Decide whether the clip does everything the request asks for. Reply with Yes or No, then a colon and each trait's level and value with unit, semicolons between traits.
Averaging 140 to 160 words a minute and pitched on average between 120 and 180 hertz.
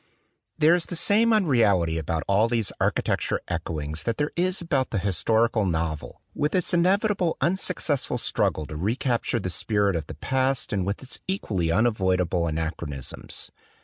No: average, 150 wpm; low, 110 Hz